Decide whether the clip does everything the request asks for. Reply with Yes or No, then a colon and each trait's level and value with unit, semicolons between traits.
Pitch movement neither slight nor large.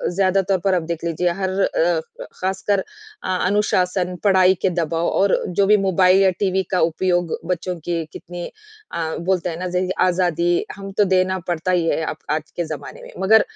No: narrow, 1.8 semitones